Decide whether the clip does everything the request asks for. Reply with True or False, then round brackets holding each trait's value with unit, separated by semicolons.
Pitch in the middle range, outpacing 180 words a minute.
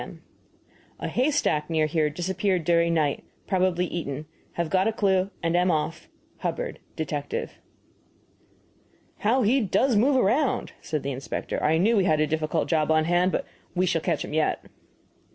False (170 Hz; 165 wpm)